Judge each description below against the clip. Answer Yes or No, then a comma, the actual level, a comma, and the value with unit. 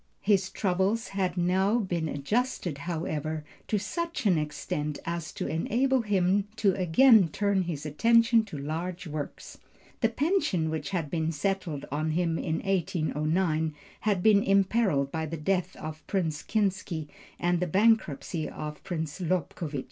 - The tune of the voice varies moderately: Yes, average, 4.2 semitones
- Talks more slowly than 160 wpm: Yes, average, 145 wpm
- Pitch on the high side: No, medium, 180 Hz